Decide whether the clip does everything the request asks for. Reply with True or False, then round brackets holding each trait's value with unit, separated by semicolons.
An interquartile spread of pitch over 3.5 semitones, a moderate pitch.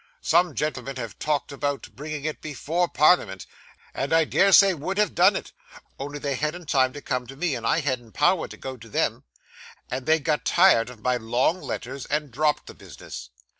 True (4.2 semitones; 145 Hz)